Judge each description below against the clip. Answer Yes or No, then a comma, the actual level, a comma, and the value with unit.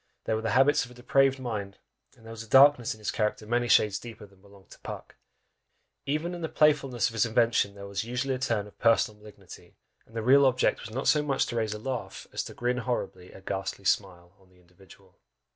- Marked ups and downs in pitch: No, average, 4.2 semitones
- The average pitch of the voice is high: No, low, 115 Hz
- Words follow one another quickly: Yes, fast, 230 wpm